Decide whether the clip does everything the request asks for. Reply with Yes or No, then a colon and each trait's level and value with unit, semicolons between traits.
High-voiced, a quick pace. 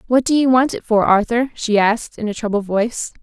Yes: high, 225 Hz; fast, 240 wpm